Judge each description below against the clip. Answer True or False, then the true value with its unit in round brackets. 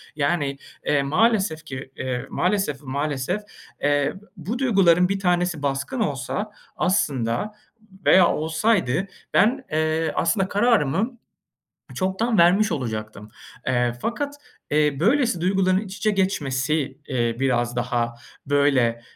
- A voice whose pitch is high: False (160 Hz)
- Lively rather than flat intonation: True (6.5 semitones)